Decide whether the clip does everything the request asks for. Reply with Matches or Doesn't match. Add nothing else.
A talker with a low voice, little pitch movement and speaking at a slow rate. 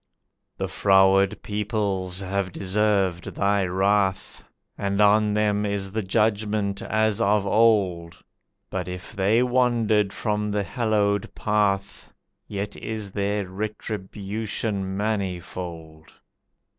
Matches